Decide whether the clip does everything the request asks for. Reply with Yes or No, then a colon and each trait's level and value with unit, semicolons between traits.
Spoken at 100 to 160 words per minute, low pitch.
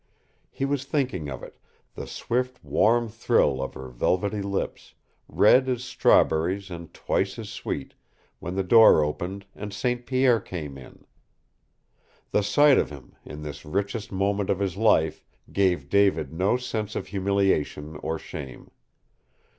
Yes: average, 145 wpm; low, 100 Hz